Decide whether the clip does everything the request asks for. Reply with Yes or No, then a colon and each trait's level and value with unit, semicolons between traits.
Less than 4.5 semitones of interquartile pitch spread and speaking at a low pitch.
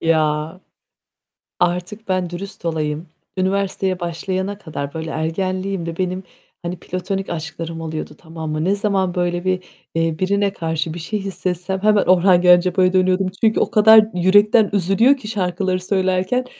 No: narrow, 2.6 semitones; medium, 185 Hz